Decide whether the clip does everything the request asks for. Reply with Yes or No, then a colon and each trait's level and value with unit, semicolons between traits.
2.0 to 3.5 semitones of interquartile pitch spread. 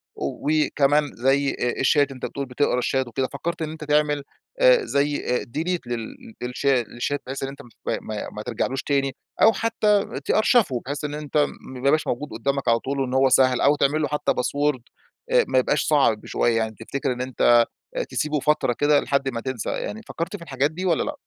Yes: average, 2.9 semitones